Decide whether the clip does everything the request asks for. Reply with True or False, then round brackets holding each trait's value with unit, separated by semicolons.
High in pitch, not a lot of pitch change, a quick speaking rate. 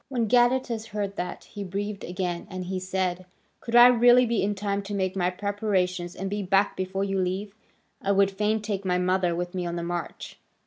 True (195 Hz; 2.3 semitones; 210 wpm)